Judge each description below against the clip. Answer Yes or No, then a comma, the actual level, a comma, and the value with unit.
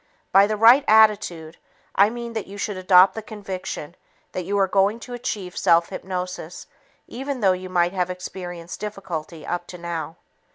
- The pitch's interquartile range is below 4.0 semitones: Yes, average, 3.1 semitones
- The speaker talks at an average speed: Yes, average, 170 wpm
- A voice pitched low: No, high, 190 Hz